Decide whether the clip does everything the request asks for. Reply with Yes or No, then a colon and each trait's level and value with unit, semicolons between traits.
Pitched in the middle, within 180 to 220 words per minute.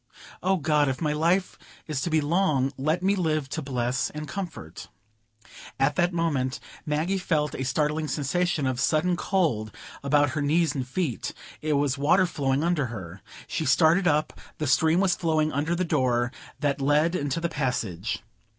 No: medium, 150 Hz; average, 170 wpm